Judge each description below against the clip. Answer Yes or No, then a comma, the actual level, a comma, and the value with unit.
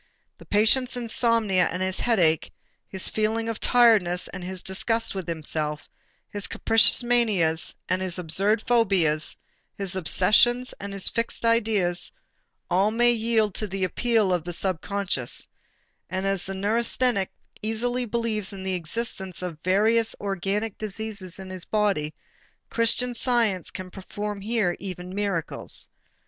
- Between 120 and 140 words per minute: Yes, slow, 135 wpm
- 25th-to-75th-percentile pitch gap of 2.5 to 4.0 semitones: Yes, average, 3.6 semitones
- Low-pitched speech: No, high, 200 Hz